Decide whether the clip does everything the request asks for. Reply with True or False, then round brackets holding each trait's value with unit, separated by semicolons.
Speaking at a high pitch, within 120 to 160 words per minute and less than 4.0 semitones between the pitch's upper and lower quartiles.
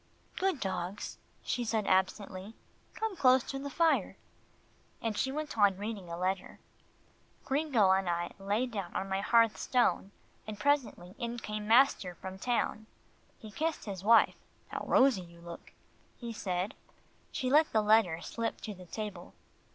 False (215 Hz; 155 wpm; 4.8 semitones)